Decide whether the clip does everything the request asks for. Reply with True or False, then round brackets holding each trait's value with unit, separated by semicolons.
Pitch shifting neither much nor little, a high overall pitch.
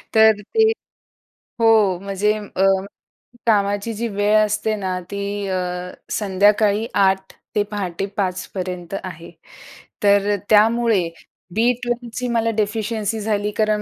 False (2.0 semitones; 205 Hz)